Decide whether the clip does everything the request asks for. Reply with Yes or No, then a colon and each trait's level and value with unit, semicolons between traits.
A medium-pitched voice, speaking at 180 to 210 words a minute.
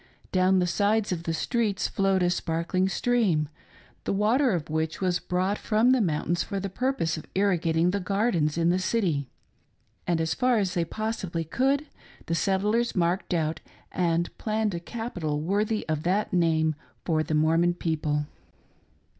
No: medium, 180 Hz; average, 170 wpm